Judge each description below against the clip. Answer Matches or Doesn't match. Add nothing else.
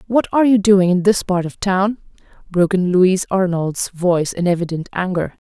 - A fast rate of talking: Doesn't match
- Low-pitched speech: Doesn't match